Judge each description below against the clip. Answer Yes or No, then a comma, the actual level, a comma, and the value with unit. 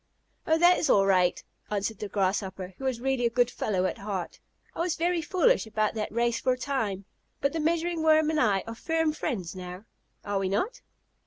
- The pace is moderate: No, fast, 210 wpm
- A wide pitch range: Yes, wide, 8.1 semitones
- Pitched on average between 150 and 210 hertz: No, high, 235 Hz